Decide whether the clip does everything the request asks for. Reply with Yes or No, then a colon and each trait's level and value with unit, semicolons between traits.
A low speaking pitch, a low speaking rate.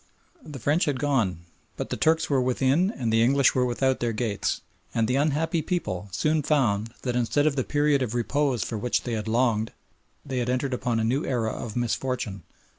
No: low, 125 Hz; average, 195 wpm